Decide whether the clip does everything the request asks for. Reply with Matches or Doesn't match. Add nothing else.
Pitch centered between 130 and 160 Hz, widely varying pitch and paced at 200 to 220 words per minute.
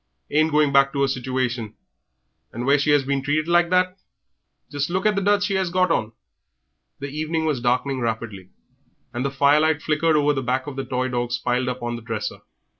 Doesn't match